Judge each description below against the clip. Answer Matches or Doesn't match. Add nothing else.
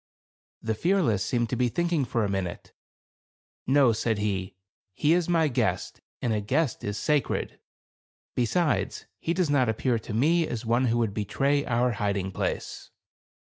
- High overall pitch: Doesn't match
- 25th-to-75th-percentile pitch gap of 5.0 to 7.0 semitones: Matches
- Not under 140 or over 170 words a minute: Matches